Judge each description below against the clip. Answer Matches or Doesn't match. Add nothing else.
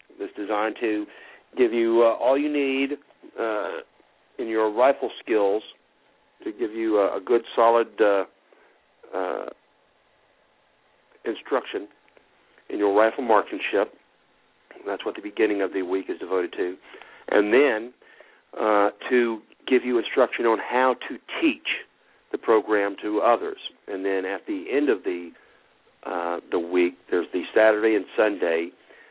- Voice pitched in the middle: Doesn't match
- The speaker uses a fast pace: Doesn't match